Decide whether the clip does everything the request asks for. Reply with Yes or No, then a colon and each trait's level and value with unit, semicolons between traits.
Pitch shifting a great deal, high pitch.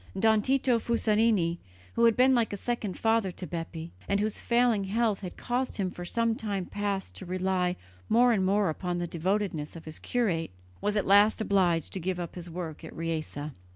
No: average, 4.2 semitones; high, 195 Hz